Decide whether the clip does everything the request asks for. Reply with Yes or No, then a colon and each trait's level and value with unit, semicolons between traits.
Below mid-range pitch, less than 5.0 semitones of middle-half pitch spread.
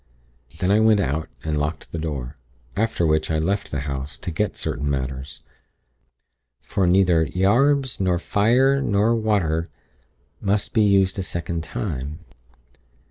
No: very low, 90 Hz; average, 5.3 semitones